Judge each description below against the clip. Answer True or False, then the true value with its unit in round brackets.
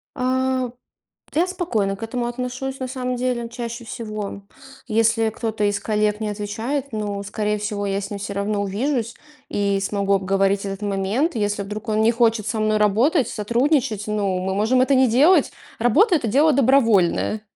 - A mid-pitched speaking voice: False (220 Hz)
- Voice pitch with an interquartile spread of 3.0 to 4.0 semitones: True (3.7 semitones)